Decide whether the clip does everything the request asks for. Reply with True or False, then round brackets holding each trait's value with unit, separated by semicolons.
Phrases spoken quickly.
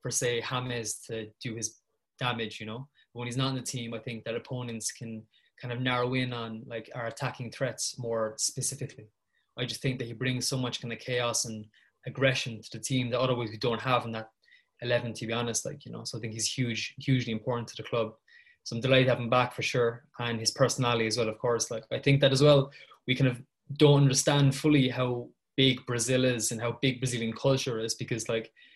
True (230 wpm)